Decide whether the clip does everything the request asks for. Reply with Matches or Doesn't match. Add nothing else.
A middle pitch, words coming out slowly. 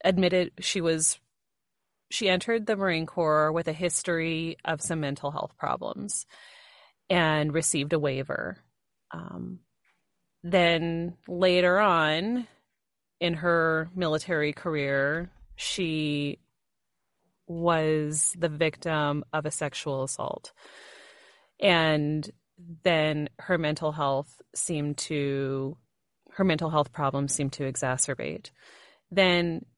Matches